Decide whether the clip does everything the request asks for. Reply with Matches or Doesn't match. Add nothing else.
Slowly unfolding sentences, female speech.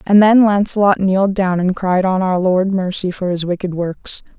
Doesn't match